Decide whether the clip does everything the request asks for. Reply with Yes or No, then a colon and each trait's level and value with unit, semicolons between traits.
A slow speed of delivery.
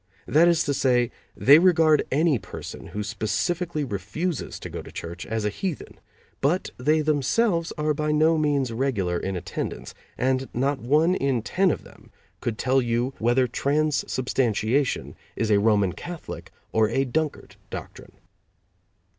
No: average, 150 wpm